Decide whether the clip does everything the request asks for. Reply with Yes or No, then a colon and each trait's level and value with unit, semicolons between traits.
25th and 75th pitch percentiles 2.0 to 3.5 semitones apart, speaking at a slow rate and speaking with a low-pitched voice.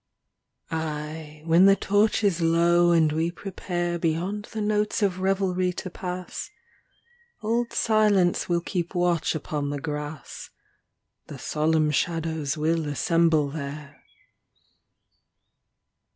No: average, 3.2 semitones; slow, 115 wpm; medium, 170 Hz